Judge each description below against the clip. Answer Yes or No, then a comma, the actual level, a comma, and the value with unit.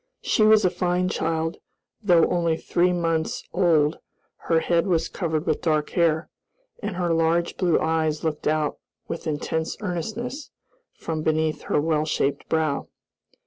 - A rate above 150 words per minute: No, average, 145 wpm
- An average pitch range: No, narrow, 2.0 semitones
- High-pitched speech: No, medium, 165 Hz